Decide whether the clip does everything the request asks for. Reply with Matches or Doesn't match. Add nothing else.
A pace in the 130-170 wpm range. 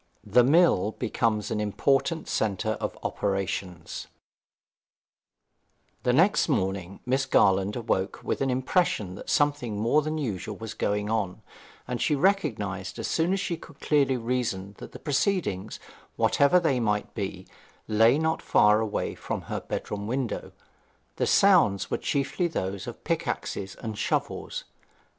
Matches